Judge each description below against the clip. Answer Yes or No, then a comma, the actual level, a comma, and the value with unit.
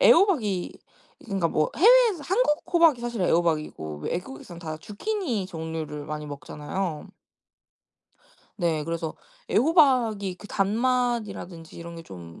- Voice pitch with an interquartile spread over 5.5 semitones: Yes, wide, 8.0 semitones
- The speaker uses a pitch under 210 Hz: Yes, high, 190 Hz